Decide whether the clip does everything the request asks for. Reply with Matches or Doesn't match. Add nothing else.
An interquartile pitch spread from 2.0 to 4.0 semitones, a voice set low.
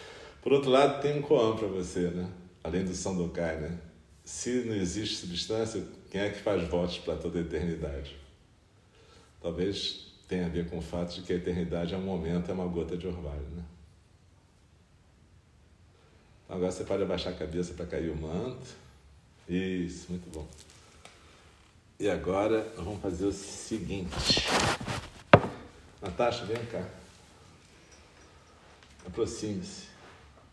Matches